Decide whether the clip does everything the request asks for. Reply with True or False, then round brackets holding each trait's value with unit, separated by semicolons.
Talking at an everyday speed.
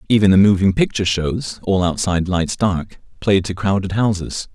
True (170 wpm)